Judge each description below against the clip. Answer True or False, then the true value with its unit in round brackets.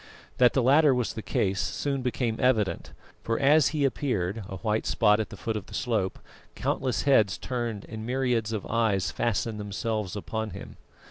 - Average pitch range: True (3.3 semitones)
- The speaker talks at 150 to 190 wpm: True (180 wpm)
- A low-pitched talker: True (115 Hz)